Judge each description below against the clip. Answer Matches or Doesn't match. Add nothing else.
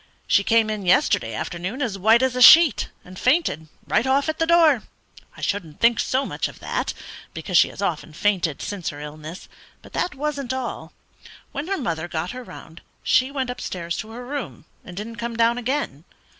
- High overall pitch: Matches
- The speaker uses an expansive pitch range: Matches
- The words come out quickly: Doesn't match